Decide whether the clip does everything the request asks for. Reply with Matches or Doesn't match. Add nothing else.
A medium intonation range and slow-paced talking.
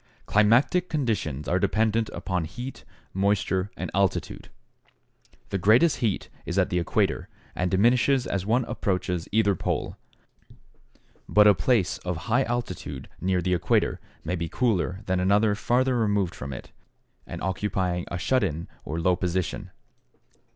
Doesn't match